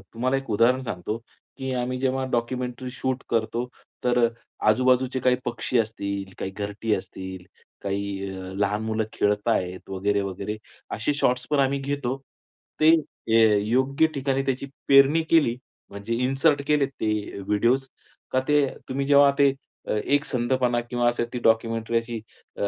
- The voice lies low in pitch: Yes, low, 120 Hz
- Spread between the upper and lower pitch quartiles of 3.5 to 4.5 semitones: Yes, average, 4.0 semitones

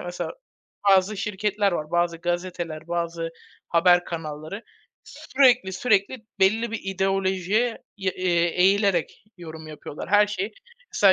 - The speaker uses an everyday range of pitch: Yes, average, 3.0 semitones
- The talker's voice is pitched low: No, medium, 185 Hz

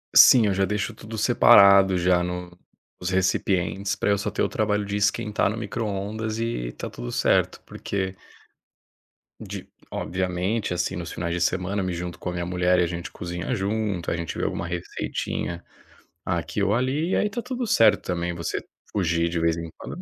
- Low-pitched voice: Yes, very low, 95 Hz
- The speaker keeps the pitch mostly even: No, average, 3.1 semitones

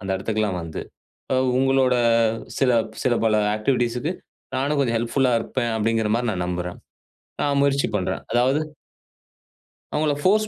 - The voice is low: Yes, low, 120 Hz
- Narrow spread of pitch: No, average, 4.2 semitones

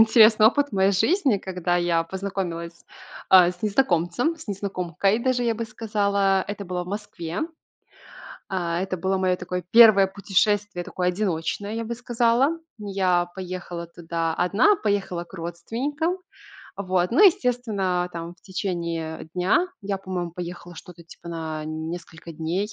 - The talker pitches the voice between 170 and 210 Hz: Yes, high, 190 Hz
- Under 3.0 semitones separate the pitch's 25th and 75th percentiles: No, average, 3.6 semitones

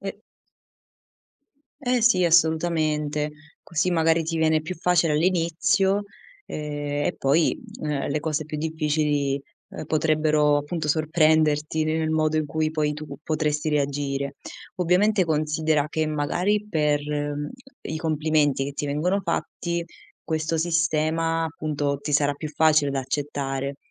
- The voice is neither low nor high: Yes, medium, 155 Hz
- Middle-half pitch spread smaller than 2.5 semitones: Yes, narrow, 1.7 semitones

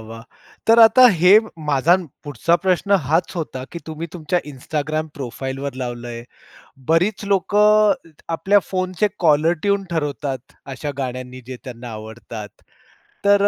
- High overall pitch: No, medium, 155 Hz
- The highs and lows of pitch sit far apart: Yes, wide, 6.4 semitones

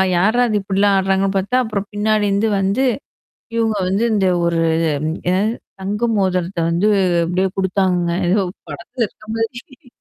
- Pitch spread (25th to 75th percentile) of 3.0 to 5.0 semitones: No, narrow, 2.5 semitones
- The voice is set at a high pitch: Yes, high, 200 Hz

